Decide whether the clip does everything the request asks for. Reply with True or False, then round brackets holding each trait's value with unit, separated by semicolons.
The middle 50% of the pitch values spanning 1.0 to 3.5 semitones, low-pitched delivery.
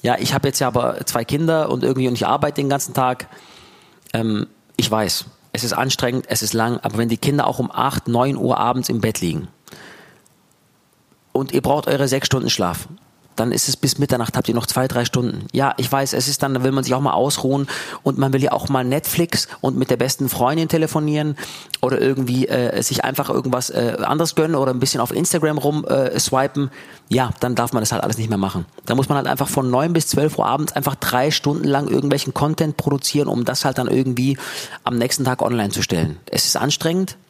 True (2.8 semitones; 130 Hz)